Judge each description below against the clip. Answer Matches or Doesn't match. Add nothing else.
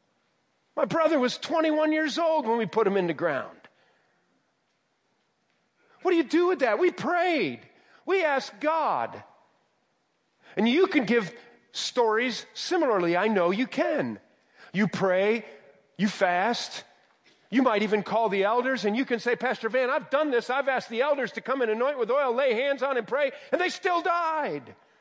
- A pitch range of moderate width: Doesn't match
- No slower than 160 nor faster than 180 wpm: Matches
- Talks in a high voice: Matches